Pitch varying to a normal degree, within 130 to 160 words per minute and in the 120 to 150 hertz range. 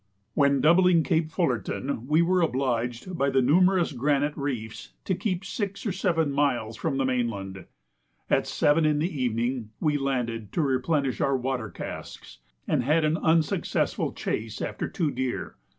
Yes: average, 4.7 semitones; average, 155 wpm; medium, 140 Hz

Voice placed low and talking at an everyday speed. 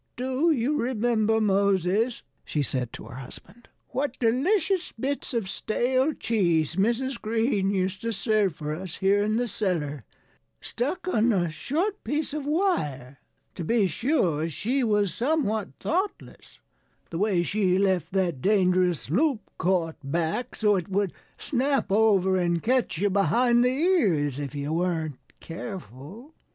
No: high, 205 Hz; average, 145 wpm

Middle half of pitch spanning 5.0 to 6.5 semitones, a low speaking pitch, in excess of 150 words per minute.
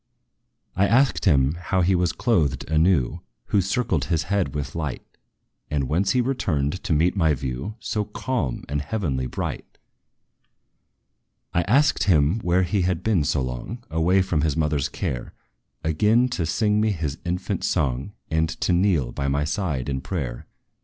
Yes: wide, 5.6 semitones; very low, 85 Hz; average, 160 wpm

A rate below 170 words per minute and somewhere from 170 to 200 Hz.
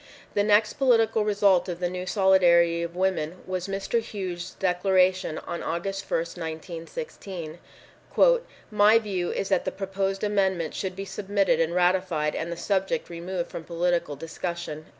Yes: average, 150 wpm; medium, 185 Hz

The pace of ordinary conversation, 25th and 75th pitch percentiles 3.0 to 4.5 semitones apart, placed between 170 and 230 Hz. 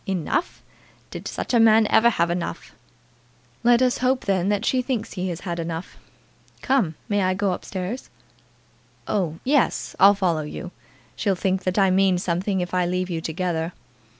Yes: average, 175 wpm; average, 3.5 semitones; high, 190 Hz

